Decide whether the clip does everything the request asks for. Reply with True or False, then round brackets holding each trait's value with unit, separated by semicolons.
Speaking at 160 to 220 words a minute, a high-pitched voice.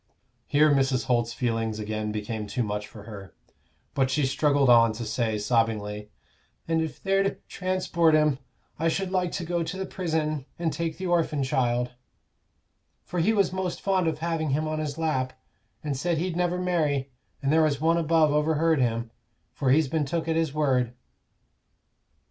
False (180 wpm; 150 Hz)